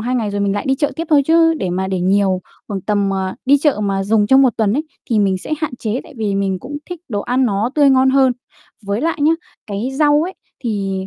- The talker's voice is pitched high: Yes, high, 220 Hz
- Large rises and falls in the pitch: Yes, wide, 5.7 semitones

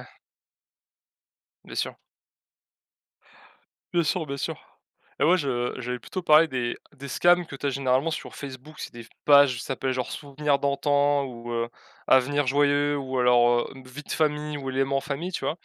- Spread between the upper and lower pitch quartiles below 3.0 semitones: Yes, narrow, 2.5 semitones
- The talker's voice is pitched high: No, medium, 140 Hz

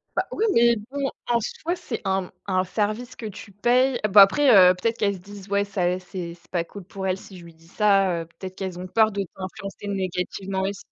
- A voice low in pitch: No, high, 195 Hz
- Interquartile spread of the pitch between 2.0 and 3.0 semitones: Yes, average, 2.7 semitones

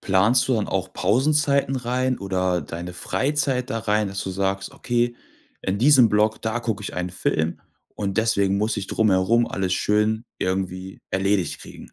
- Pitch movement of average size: Yes, average, 4.0 semitones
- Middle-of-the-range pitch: No, low, 105 Hz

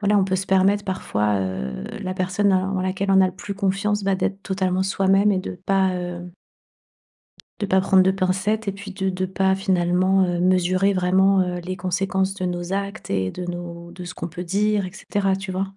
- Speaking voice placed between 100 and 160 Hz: No, high, 190 Hz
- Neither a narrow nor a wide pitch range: No, narrow, 1.4 semitones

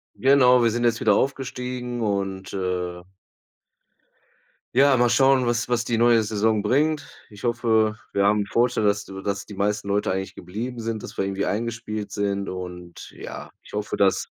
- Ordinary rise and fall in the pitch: Yes, average, 3.4 semitones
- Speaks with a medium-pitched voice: No, low, 110 Hz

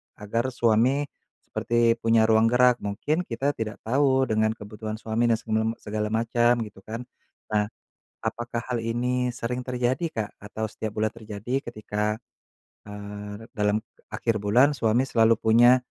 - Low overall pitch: Yes, low, 115 Hz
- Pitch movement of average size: No, narrow, 2.2 semitones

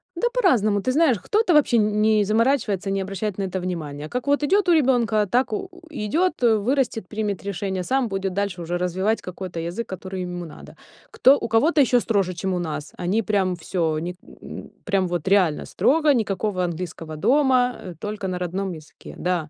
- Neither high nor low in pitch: No, high, 200 Hz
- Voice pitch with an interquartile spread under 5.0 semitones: No, average, 5.3 semitones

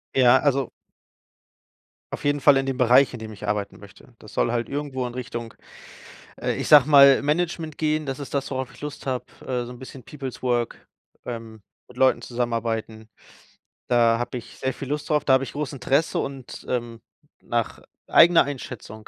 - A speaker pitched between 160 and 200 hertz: No, low, 130 Hz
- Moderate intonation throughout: Yes, average, 3.0 semitones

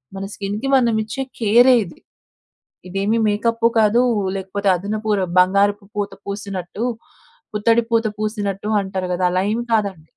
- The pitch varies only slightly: Yes, narrow, 2.3 semitones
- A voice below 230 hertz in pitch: Yes, high, 205 Hz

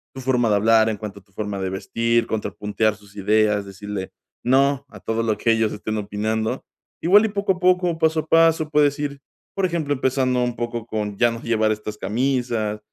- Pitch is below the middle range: Yes, low, 115 Hz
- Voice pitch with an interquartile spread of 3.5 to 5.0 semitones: Yes, average, 4.7 semitones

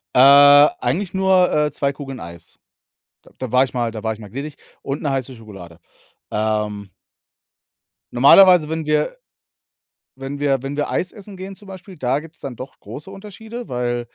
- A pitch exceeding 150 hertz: No, medium, 140 Hz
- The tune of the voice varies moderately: No, wide, 6.9 semitones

